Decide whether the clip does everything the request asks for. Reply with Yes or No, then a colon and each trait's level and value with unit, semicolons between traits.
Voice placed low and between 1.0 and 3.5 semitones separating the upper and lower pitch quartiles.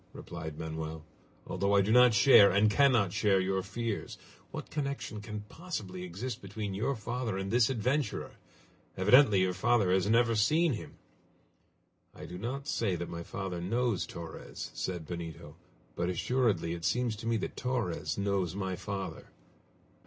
No: low, 100 Hz; average, 4.7 semitones